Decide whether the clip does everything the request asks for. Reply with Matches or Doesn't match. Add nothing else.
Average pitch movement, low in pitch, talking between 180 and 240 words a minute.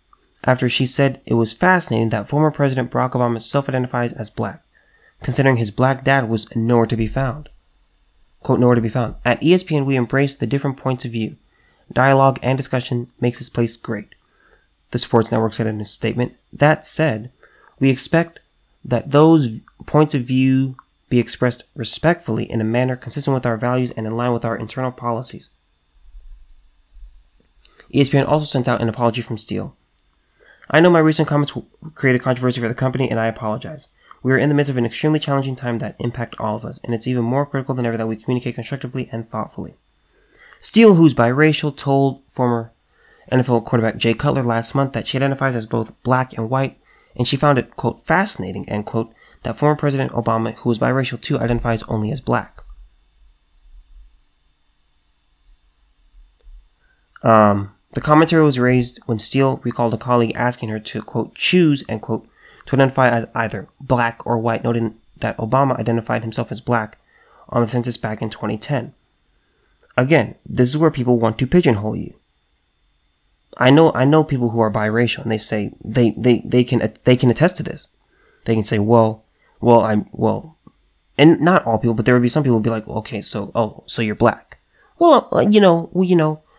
Matches